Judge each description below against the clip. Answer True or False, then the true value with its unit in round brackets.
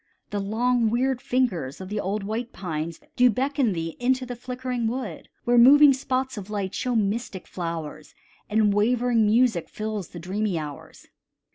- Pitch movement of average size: True (4.7 semitones)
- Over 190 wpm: False (160 wpm)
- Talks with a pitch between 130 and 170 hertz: False (220 Hz)